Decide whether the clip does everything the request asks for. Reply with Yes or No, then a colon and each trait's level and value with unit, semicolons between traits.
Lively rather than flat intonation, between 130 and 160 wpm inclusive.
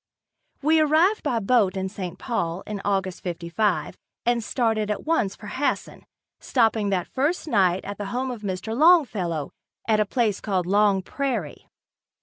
No: average, 4.7 semitones; average, 155 wpm